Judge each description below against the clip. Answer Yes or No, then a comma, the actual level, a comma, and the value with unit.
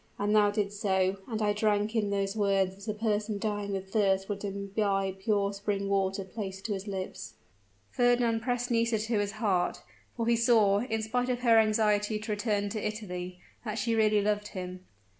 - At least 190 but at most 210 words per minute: Yes, average, 195 wpm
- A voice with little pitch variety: Yes, narrow, 1.9 semitones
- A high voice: Yes, high, 210 Hz